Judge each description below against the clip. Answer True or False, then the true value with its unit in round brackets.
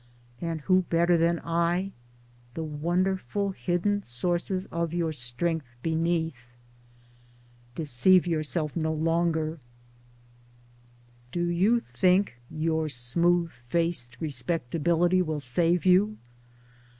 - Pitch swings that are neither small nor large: False (2.1 semitones)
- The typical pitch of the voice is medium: True (170 Hz)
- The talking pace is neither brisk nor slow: False (95 wpm)